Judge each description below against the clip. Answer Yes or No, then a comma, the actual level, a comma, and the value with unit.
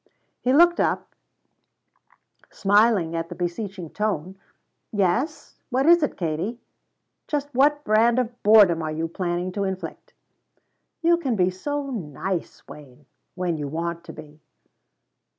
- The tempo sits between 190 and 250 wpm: No, slow, 135 wpm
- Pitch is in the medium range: No, high, 195 Hz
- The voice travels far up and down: Yes, wide, 6.7 semitones